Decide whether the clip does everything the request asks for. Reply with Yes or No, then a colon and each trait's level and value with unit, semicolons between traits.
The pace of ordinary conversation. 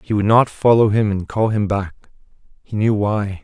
No: fast, 210 wpm